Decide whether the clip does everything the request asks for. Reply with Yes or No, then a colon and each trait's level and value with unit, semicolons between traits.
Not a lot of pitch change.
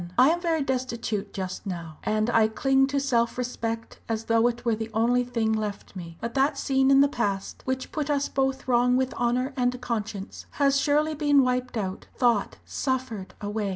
No: average, 3.5 semitones